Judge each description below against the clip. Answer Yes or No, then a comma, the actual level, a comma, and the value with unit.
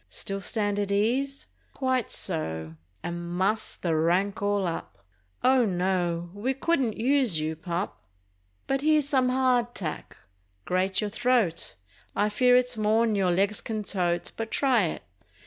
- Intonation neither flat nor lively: No, wide, 6.0 semitones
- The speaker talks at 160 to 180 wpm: No, average, 145 wpm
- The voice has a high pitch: Yes, high, 205 Hz